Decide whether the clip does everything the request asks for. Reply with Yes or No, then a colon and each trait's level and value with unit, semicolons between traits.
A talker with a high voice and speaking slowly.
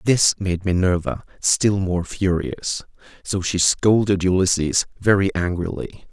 No: very low, 90 Hz; slow, 120 wpm